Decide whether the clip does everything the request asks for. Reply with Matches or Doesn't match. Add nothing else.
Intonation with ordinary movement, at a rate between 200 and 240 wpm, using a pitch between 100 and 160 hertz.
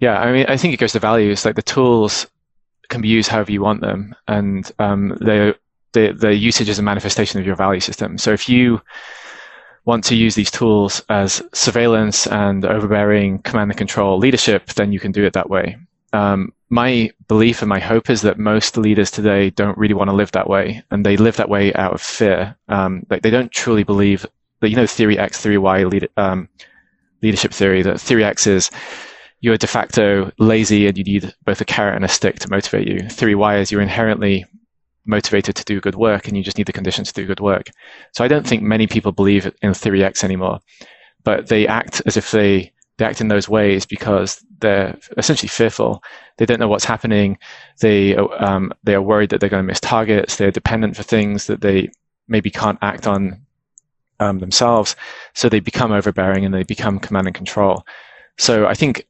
Doesn't match